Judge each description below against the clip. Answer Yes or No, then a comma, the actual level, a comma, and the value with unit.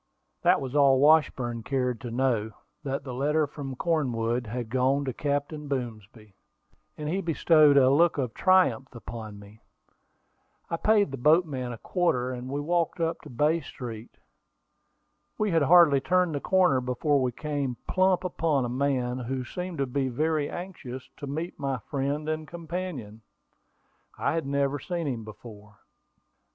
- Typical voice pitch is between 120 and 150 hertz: Yes, medium, 140 Hz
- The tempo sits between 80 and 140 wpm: No, average, 160 wpm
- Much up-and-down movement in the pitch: No, average, 4.2 semitones